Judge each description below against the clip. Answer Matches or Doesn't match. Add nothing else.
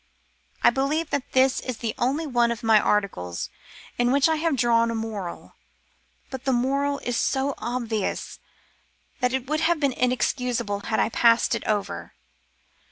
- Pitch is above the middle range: Matches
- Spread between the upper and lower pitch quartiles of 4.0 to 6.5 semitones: Doesn't match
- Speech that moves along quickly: Doesn't match